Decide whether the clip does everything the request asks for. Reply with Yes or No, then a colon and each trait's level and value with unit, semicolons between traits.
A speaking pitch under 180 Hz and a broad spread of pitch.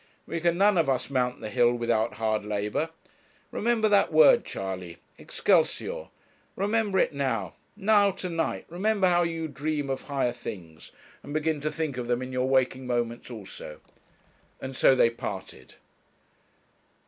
Yes: low, 135 Hz; wide, 6.5 semitones